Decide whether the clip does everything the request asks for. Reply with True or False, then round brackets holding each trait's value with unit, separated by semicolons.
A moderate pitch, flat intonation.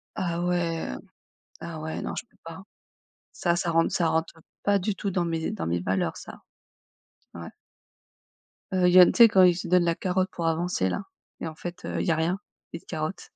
True (170 Hz; 1.9 semitones)